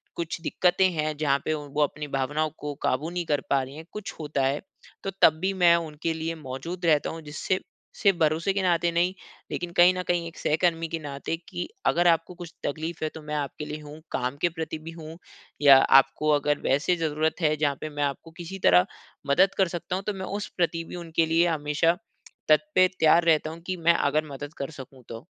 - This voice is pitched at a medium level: Yes, medium, 160 Hz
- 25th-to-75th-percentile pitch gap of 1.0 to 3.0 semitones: Yes, narrow, 2.6 semitones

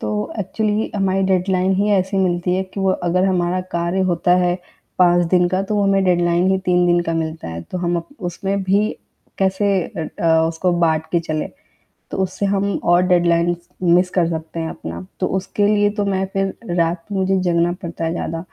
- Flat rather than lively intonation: Yes, narrow, 2.0 semitones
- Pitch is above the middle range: No, medium, 180 Hz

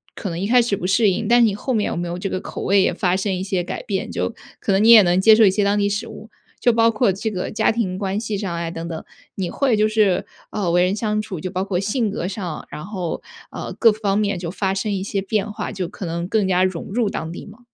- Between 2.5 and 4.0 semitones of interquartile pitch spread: Yes, average, 2.8 semitones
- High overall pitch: Yes, high, 200 Hz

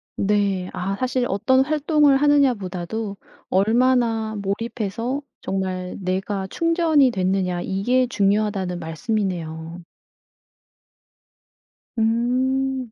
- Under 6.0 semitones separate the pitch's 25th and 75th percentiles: Yes, average, 5.1 semitones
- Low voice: No, high, 215 Hz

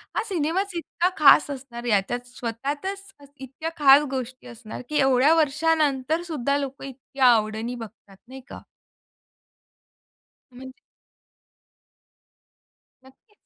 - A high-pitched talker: Yes, very high, 270 Hz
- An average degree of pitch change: Yes, average, 3.7 semitones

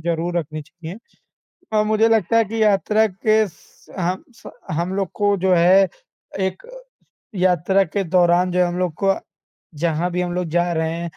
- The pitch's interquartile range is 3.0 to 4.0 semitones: No, narrow, 2.4 semitones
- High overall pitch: No, medium, 180 Hz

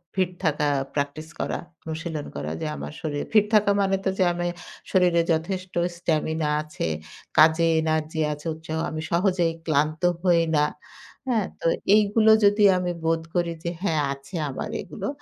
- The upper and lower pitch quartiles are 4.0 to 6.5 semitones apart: No, average, 3.0 semitones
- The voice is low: No, medium, 165 Hz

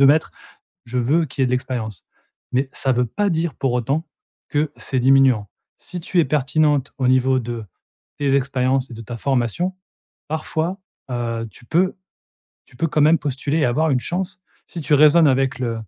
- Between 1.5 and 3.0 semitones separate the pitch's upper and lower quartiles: No, average, 3.9 semitones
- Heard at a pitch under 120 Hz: No, low, 135 Hz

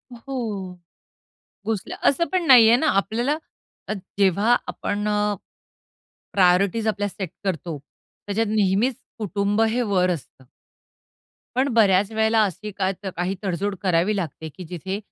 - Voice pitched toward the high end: Yes, high, 205 Hz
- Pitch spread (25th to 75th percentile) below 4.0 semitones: Yes, average, 3.1 semitones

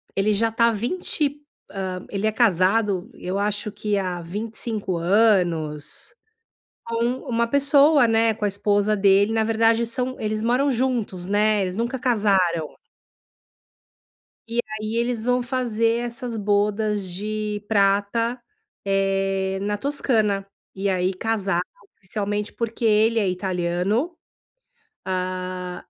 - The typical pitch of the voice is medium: No, high, 210 Hz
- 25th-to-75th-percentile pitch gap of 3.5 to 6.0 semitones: No, average, 3.0 semitones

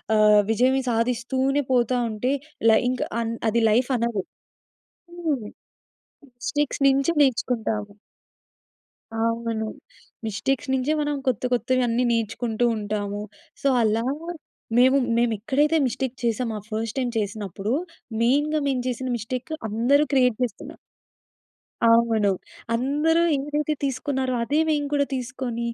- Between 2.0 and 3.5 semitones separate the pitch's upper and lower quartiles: Yes, average, 3.1 semitones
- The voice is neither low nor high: No, high, 245 Hz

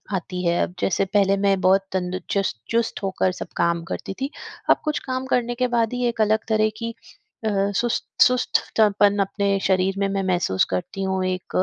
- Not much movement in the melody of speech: No, average, 3.0 semitones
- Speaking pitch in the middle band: No, high, 195 Hz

